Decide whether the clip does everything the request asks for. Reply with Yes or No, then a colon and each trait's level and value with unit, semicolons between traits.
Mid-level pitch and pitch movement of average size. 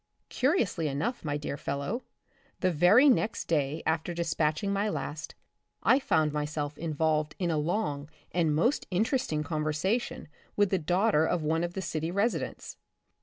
Yes: medium, 165 Hz; average, 4.7 semitones